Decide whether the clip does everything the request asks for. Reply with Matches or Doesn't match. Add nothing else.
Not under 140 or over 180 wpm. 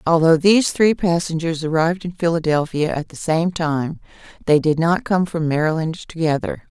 Matches